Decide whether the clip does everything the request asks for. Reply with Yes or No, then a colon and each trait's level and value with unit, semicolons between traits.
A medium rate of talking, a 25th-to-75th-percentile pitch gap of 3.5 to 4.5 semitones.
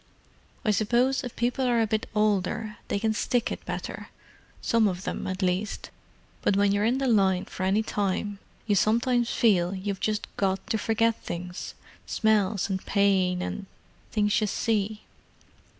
No: average, 150 wpm; narrow, 2.6 semitones